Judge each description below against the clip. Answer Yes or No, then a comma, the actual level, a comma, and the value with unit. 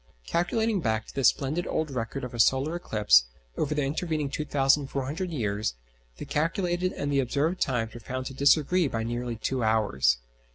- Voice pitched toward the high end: No, low, 135 Hz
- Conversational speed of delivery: Yes, average, 170 wpm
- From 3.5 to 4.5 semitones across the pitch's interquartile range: No, average, 5.2 semitones